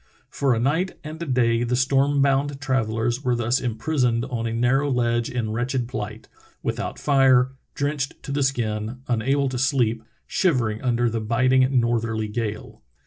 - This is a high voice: No, low, 125 Hz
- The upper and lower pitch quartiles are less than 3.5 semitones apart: Yes, average, 2.7 semitones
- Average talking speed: Yes, average, 170 wpm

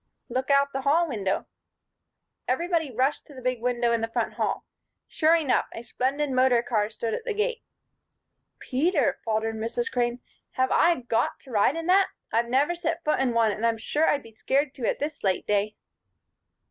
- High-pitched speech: Yes, very high, 260 Hz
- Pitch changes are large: No, average, 4.9 semitones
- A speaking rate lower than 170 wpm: No, average, 190 wpm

